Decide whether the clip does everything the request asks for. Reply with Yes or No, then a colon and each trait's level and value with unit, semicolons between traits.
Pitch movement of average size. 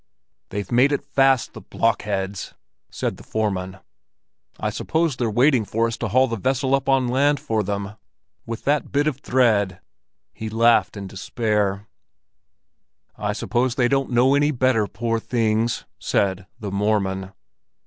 Yes: average, 4.1 semitones